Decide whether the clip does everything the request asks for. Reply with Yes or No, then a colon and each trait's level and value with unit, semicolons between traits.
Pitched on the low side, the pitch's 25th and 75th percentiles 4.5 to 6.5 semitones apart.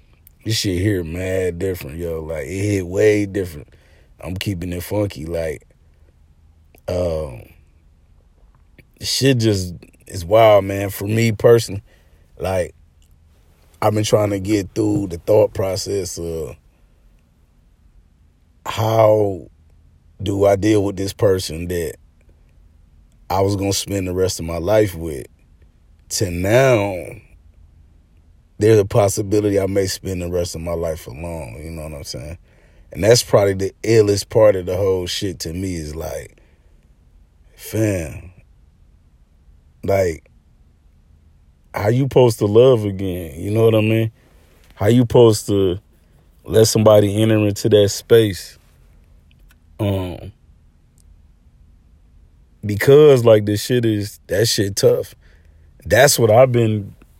Yes: very low, 90 Hz; average, 4.8 semitones